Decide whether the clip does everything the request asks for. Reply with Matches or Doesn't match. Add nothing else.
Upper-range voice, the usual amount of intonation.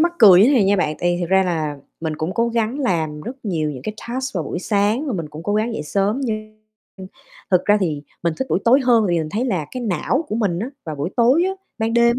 Doesn't match